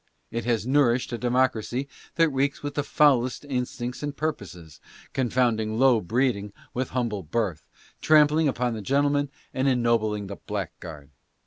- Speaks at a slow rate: No, average, 150 wpm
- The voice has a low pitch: Yes, low, 125 Hz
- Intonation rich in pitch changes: No, average, 4.1 semitones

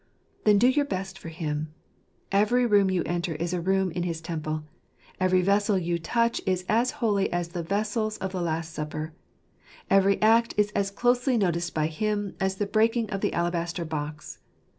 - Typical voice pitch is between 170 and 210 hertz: Yes, high, 190 Hz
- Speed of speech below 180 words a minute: No, average, 185 wpm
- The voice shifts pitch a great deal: No, average, 3.8 semitones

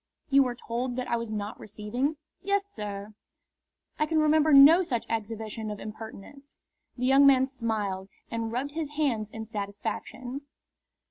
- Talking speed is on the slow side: No, average, 150 wpm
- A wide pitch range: No, average, 4.6 semitones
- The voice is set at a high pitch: Yes, high, 240 Hz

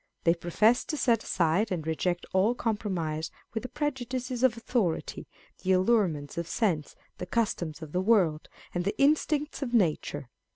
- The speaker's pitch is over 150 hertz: Yes, high, 190 Hz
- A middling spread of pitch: No, wide, 6.2 semitones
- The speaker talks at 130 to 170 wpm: Yes, average, 160 wpm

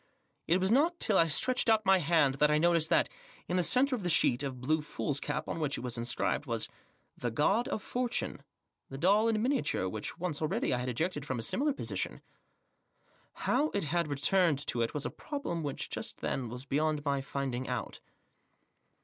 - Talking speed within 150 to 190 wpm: No, average, 200 wpm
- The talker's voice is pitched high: No, medium, 155 Hz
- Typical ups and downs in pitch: No, wide, 6.5 semitones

